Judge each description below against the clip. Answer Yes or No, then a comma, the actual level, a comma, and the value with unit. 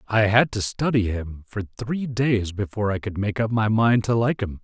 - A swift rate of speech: Yes, fast, 235 wpm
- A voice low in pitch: Yes, low, 110 Hz